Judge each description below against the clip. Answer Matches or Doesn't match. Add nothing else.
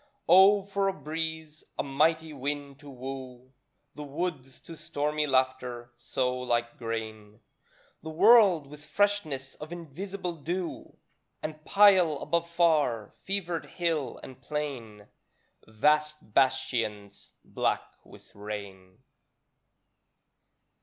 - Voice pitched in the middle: Matches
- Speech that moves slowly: Matches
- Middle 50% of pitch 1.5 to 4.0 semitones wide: Doesn't match